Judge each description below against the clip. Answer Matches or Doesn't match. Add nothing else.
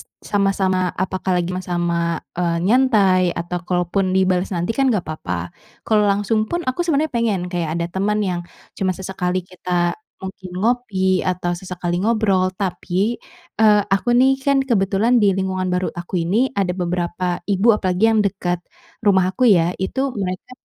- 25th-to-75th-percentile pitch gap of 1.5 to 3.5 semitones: Matches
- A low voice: Doesn't match